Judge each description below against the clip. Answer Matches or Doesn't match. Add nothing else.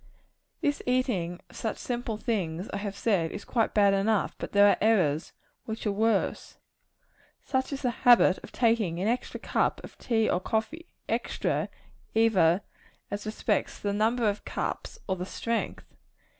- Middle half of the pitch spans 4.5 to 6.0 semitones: Doesn't match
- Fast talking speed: Doesn't match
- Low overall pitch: Doesn't match